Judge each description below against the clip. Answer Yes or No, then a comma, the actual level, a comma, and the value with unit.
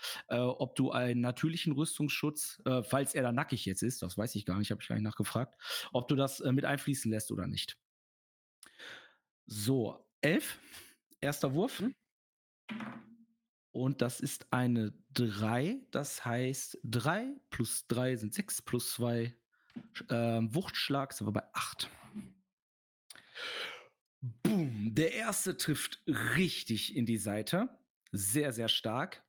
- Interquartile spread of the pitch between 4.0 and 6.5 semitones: Yes, average, 5.3 semitones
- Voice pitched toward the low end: Yes, low, 130 Hz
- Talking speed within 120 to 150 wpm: Yes, average, 135 wpm